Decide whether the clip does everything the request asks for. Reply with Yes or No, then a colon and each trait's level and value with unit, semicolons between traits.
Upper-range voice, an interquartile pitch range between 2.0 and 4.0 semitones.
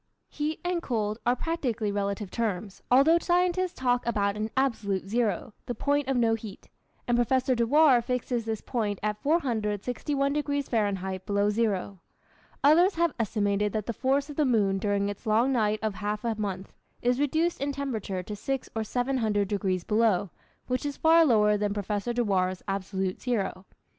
No: high, 225 Hz; average, 4.9 semitones